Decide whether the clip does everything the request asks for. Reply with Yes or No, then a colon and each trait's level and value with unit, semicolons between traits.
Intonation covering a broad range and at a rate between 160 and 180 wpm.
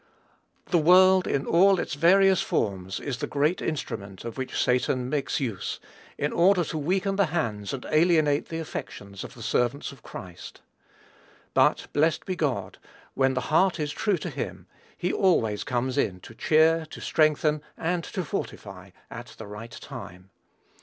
Yes: wide, 6.6 semitones; average, 165 wpm